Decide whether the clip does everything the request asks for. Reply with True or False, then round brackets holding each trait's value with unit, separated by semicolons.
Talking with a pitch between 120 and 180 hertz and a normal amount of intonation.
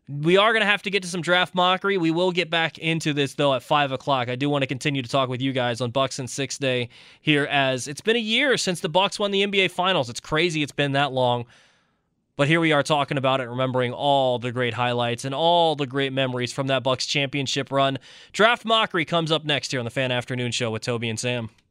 True (140 Hz; 4.6 semitones)